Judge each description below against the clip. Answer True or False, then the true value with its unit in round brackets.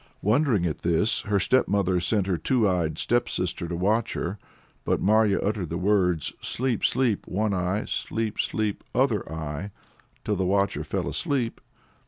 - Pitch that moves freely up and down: False (3.5 semitones)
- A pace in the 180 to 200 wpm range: False (155 wpm)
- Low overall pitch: True (100 Hz)